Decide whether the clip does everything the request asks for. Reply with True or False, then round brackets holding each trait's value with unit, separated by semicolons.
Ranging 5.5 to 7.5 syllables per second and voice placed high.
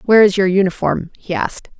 True (5.9 syllables/s; 195 Hz)